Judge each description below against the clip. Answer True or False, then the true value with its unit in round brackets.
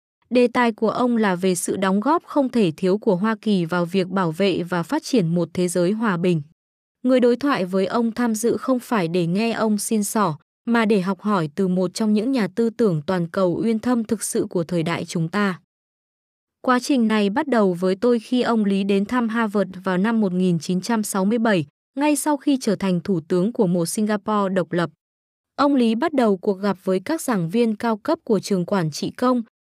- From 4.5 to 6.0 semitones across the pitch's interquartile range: False (4.1 semitones)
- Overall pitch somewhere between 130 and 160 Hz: False (210 Hz)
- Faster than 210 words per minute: True (220 wpm)